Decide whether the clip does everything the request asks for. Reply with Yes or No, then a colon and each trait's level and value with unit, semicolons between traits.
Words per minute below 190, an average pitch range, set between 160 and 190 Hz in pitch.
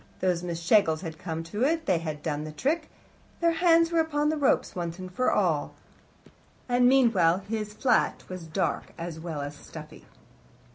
No: average, 180 wpm; wide, 8.1 semitones; medium, 185 Hz